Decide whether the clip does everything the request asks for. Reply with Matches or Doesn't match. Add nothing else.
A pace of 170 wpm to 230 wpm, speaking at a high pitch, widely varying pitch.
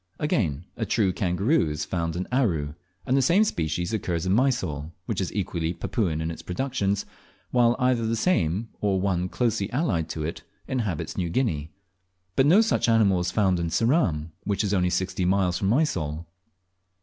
Doesn't match